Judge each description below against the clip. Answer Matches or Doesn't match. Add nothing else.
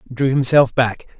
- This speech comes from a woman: Doesn't match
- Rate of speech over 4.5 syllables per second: Doesn't match